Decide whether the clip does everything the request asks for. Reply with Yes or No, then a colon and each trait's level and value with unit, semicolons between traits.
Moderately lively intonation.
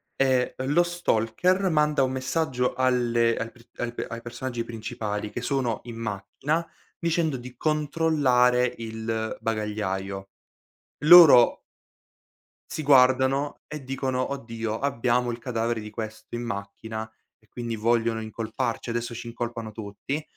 Yes: average, 3.1 semitones